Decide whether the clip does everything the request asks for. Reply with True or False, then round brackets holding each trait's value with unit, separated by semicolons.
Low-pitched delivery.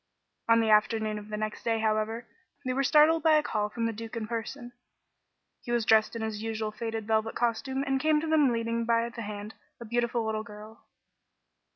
False (230 Hz)